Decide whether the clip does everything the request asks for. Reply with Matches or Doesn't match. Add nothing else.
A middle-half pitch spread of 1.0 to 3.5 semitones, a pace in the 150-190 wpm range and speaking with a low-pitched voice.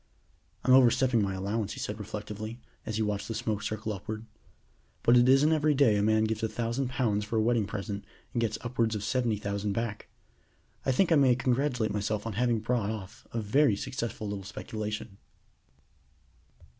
Matches